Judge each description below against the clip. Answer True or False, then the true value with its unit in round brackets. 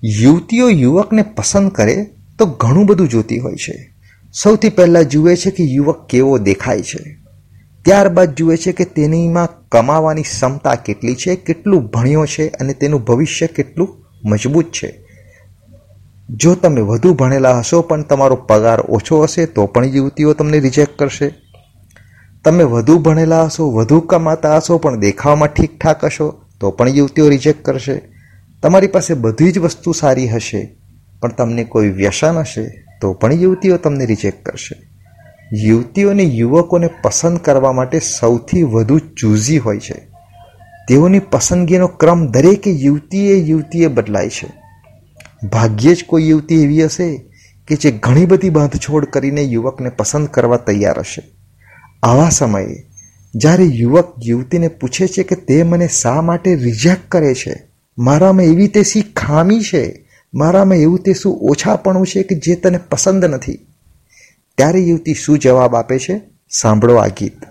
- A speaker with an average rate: False (145 wpm)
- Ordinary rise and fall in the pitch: False (6.6 semitones)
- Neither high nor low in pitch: True (150 Hz)